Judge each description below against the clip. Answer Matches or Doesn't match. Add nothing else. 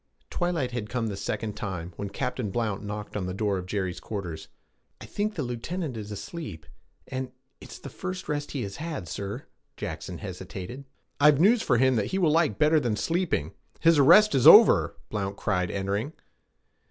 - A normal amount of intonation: Doesn't match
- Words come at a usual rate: Matches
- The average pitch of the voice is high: Doesn't match